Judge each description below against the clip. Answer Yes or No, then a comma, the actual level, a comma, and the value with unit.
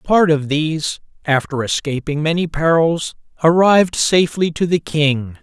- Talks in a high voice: No, medium, 160 Hz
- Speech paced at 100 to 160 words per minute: Yes, slow, 135 wpm